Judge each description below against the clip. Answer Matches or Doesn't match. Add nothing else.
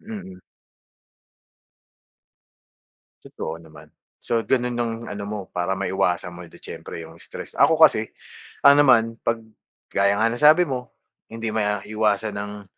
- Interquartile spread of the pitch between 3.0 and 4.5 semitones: Matches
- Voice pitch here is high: Doesn't match